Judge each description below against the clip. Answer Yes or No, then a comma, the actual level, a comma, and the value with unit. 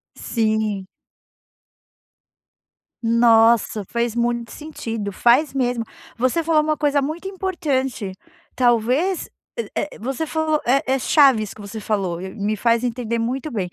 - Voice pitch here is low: No, high, 240 Hz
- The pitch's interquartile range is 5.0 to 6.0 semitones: No, average, 4.6 semitones